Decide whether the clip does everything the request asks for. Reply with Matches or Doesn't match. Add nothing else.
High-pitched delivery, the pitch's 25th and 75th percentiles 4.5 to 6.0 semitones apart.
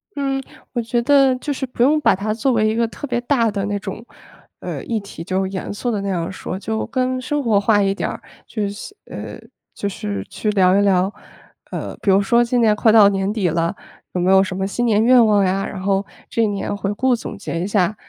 Doesn't match